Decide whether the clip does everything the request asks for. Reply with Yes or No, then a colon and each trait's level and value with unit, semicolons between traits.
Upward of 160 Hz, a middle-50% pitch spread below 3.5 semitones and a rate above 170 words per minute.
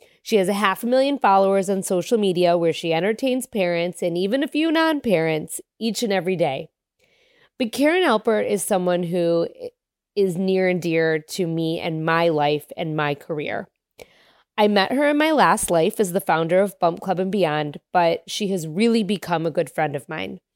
No: high, 190 Hz; average, 5.1 semitones; average, 195 wpm